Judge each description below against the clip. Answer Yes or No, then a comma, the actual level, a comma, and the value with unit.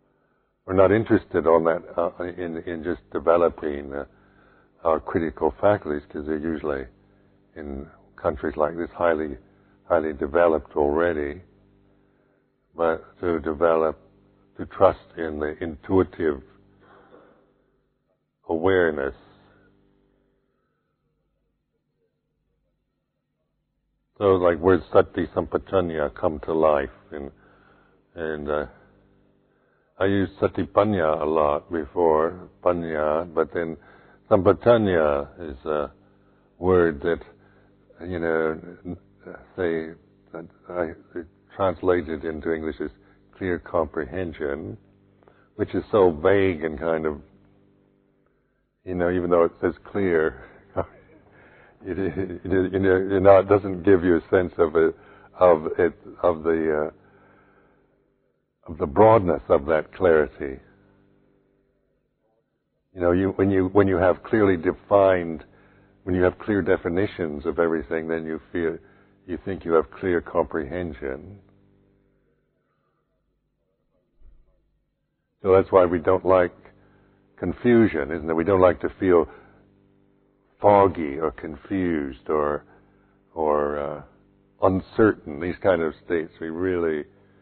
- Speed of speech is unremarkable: No, slow, 110 wpm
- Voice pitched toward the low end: Yes, very low, 95 Hz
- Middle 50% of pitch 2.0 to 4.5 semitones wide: Yes, average, 3.4 semitones